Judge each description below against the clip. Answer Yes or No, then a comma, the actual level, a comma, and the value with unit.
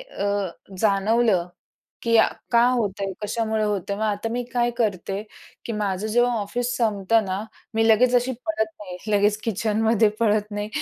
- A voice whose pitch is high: Yes, high, 215 Hz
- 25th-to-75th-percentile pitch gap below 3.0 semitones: Yes, narrow, 2.4 semitones